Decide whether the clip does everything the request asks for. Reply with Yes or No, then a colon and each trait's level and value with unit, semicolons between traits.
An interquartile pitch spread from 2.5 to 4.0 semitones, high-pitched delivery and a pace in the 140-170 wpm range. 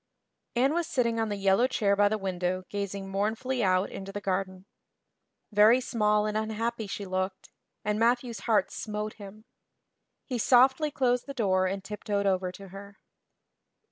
Yes: average, 3.1 semitones; high, 210 Hz; average, 160 wpm